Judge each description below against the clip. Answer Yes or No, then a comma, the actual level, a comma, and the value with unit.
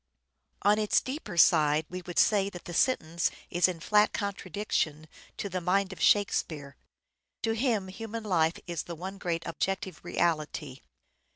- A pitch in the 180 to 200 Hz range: Yes, medium, 185 Hz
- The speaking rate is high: No, average, 155 wpm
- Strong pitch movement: No, average, 3.7 semitones